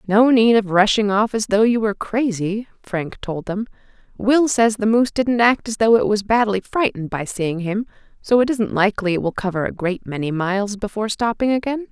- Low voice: No, high, 215 Hz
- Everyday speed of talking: No, fast, 210 wpm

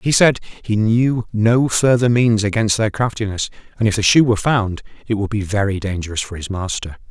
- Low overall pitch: Yes, low, 110 Hz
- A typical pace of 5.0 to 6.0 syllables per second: Yes, 5.3 syllables/s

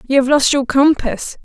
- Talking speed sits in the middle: No, fast, 210 wpm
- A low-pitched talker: No, very high, 270 Hz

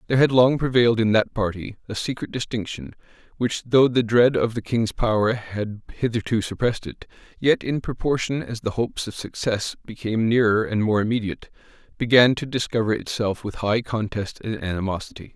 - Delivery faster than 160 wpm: Yes, average, 170 wpm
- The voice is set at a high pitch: No, low, 115 Hz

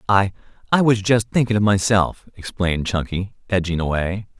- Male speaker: Yes, male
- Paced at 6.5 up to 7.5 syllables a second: No, 5.2 syllables/s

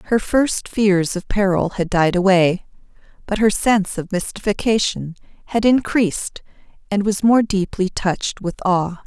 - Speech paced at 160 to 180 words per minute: No, average, 145 wpm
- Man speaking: No, female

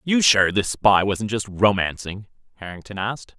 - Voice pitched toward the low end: Yes, low, 105 Hz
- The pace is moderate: Yes, average, 160 wpm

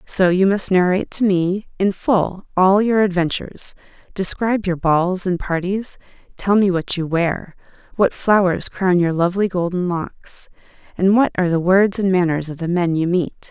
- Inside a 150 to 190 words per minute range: Yes, average, 180 wpm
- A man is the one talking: No, female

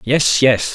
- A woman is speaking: No, male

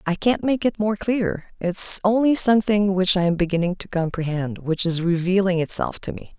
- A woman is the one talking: Yes, female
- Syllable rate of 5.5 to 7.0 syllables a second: No, 5.1 syllables/s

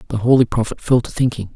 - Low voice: Yes, low, 120 Hz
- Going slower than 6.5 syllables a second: No, 6.8 syllables/s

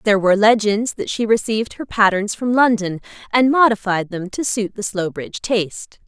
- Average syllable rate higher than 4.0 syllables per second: Yes, 5.4 syllables/s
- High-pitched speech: Yes, high, 210 Hz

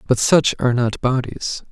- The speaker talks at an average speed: Yes, average, 175 wpm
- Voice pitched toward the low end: Yes, low, 125 Hz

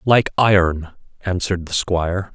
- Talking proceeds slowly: Yes, slow, 130 wpm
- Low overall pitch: Yes, very low, 90 Hz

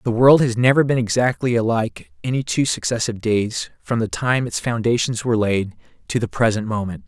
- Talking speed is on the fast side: No, average, 185 wpm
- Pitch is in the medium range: No, low, 115 Hz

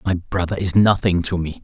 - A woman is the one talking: No, male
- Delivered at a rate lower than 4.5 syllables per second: No, 5.2 syllables/s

